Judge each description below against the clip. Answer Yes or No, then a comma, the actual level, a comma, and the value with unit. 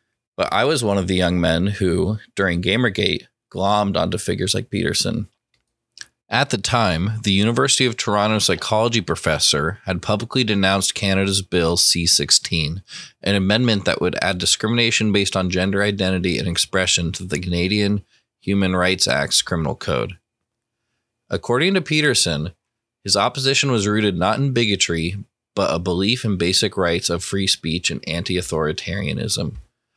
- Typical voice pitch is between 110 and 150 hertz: No, low, 100 Hz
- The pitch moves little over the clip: No, average, 3.9 semitones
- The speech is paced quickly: No, average, 150 wpm